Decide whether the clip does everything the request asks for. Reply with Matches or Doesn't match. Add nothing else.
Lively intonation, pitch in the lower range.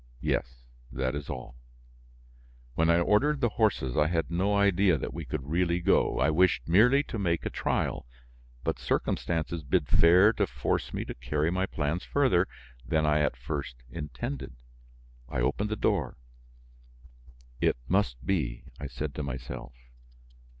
Matches